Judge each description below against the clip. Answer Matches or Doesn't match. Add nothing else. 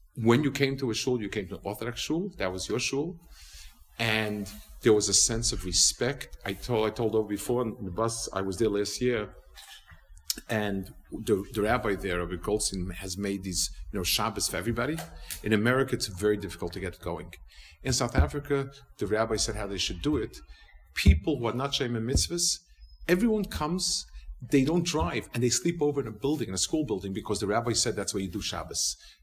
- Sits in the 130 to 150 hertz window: Doesn't match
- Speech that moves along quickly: Matches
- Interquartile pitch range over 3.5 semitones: Matches